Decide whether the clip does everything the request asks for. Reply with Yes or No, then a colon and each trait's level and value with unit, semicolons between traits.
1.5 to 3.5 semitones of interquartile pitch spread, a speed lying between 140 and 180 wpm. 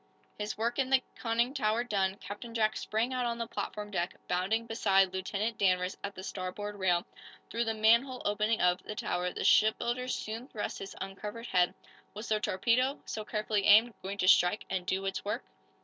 No: average, 3.1 semitones; average, 190 wpm